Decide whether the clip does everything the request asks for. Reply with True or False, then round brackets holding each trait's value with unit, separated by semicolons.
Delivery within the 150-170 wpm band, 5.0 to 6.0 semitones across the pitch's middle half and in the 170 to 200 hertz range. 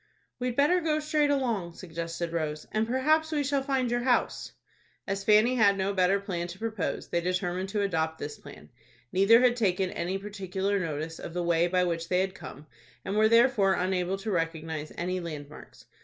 False (190 wpm; 5.3 semitones; 190 Hz)